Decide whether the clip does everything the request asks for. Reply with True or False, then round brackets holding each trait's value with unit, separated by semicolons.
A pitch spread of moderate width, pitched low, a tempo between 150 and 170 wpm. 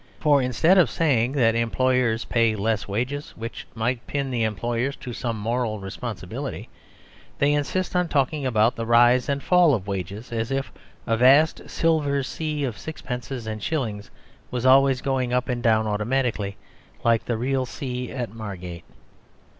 True (3.5 semitones; 125 Hz; 160 wpm)